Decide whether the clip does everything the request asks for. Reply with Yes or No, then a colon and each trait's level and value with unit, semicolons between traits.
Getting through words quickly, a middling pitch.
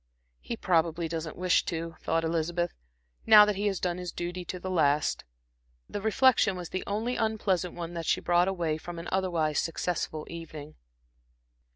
No: average, 170 wpm; medium, 175 Hz